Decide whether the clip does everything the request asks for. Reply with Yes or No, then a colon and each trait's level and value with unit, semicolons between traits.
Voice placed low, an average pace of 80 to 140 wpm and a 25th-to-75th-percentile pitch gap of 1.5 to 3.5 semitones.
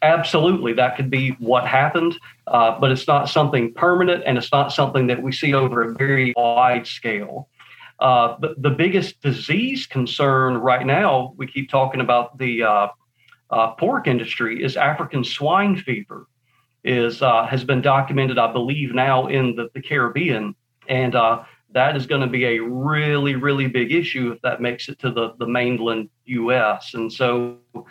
No: low, 130 Hz; average, 170 wpm; average, 2.7 semitones